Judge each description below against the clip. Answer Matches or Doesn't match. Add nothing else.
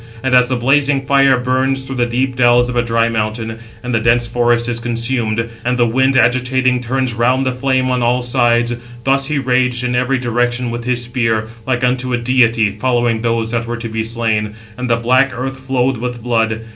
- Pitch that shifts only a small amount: Matches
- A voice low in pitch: Matches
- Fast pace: Matches